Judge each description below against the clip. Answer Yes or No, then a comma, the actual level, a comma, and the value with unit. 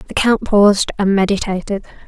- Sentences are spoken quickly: No, average, 145 wpm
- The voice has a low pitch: No, high, 200 Hz